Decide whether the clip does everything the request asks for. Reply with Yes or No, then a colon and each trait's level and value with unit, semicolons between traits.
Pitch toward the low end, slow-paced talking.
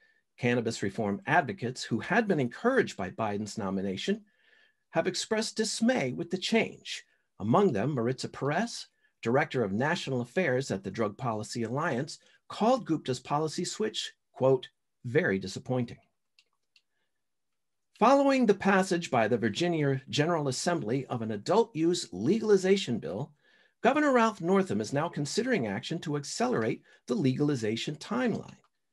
No: medium, 160 Hz; slow, 130 wpm